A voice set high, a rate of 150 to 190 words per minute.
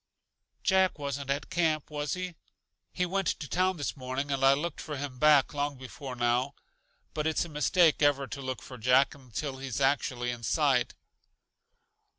No: medium, 140 Hz; average, 170 wpm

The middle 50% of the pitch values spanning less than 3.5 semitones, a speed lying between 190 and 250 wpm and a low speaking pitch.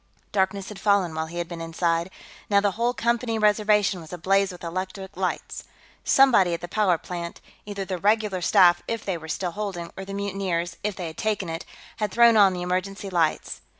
No: average, 3.0 semitones; average, 200 wpm; high, 190 Hz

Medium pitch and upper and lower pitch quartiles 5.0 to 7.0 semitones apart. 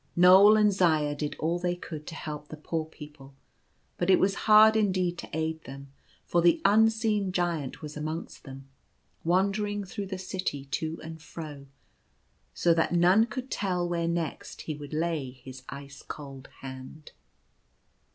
No: medium, 165 Hz; average, 4.1 semitones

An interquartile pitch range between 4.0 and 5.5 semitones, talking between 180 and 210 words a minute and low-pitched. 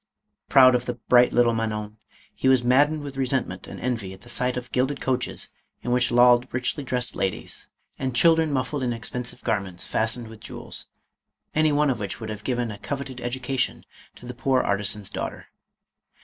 No: average, 2.7 semitones; average, 190 wpm; low, 125 Hz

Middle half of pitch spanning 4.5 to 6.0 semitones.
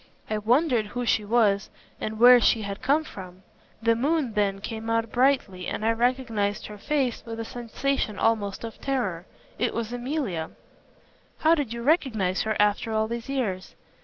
No: average, 3.3 semitones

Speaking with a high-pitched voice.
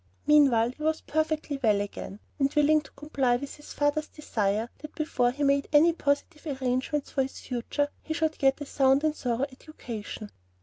Yes: very high, 280 Hz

